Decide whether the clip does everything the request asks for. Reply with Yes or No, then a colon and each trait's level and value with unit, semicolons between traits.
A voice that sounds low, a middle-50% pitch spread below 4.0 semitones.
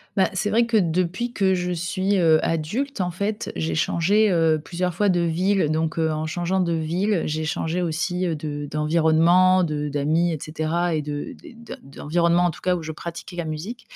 No: medium, 170 Hz; average, 2.7 semitones